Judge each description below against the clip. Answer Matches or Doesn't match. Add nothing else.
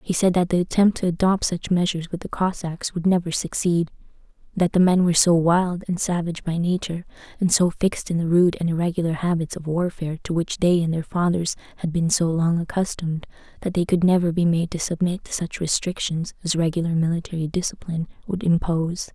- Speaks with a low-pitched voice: Doesn't match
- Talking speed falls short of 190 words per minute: Doesn't match